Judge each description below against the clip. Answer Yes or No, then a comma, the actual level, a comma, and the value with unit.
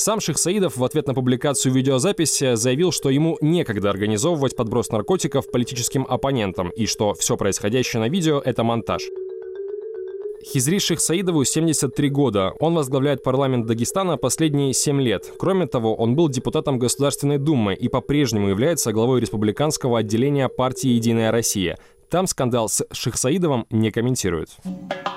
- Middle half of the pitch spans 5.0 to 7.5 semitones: Yes, wide, 5.4 semitones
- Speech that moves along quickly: No, average, 135 wpm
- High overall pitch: No, low, 135 Hz